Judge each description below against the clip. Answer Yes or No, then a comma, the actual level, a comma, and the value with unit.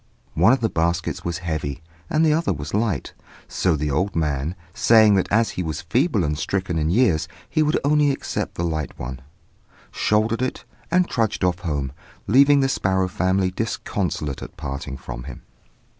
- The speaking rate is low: No, average, 175 wpm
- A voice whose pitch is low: Yes, very low, 95 Hz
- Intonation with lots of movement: Yes, wide, 6.6 semitones